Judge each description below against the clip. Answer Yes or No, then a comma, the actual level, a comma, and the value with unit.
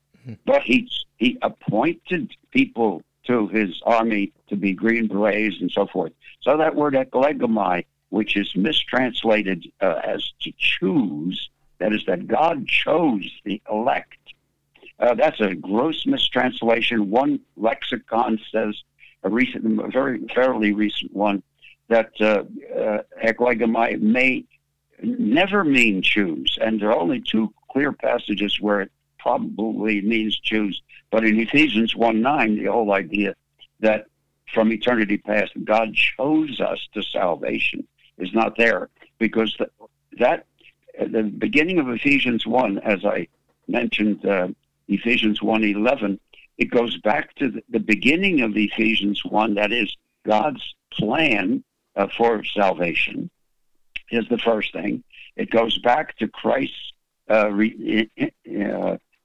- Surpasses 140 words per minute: No, slow, 135 wpm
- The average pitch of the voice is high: No, low, 110 Hz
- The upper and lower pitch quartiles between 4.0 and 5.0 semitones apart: No, average, 3.3 semitones